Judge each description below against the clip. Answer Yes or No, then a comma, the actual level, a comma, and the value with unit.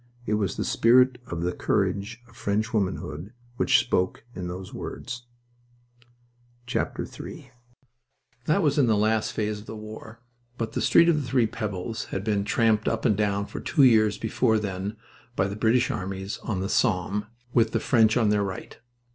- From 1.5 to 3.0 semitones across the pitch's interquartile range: Yes, narrow, 2.5 semitones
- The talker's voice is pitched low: Yes, low, 110 Hz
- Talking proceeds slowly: No, average, 175 wpm